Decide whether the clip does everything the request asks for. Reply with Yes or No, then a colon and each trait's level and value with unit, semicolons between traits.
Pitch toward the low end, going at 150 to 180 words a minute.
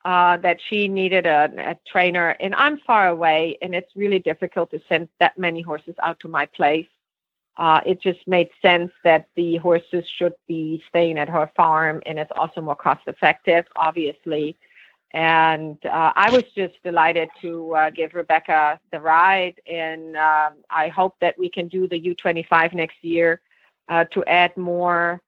No: medium, 170 Hz; average, 175 wpm